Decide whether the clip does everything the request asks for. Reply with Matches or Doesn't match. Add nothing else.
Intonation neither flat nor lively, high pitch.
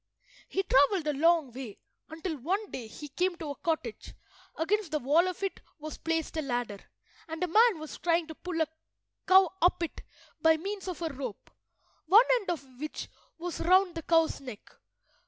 Matches